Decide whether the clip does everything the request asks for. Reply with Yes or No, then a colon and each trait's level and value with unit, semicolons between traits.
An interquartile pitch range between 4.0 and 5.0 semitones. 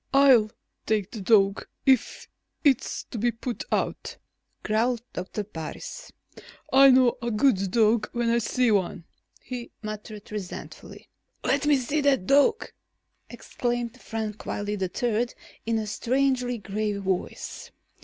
No: average, 3.2 semitones